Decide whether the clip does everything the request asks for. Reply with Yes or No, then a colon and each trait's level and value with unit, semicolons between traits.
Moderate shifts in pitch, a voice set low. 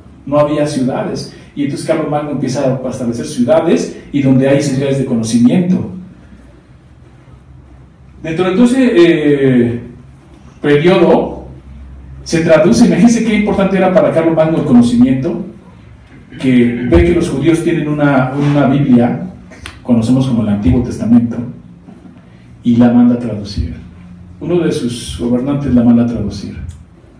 No: wide, 7.2 semitones; low, 130 Hz